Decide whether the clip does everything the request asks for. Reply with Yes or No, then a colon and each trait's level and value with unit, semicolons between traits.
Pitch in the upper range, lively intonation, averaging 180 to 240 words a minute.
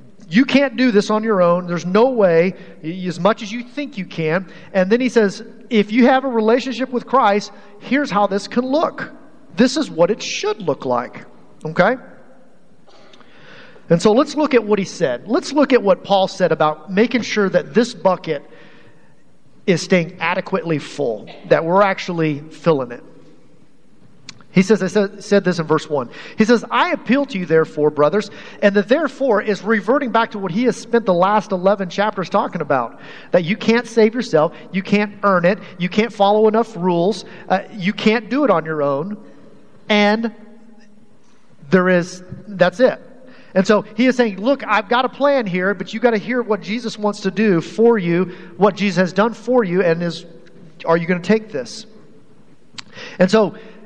No: high, 205 Hz; average, 4.2 semitones; average, 190 wpm